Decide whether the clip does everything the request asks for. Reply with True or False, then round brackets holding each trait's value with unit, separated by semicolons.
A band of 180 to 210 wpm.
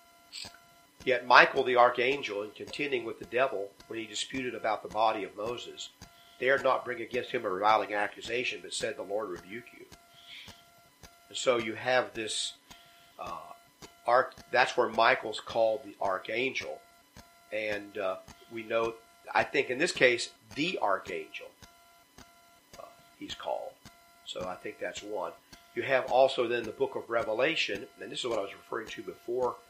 False (160 wpm)